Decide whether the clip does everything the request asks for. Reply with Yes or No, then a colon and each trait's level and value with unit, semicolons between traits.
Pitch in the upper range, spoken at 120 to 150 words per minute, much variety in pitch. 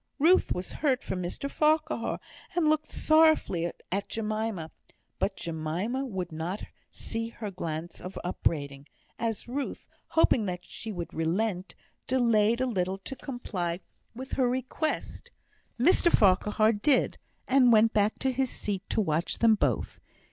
Yes: high, 215 Hz; average, 140 wpm; wide, 6.3 semitones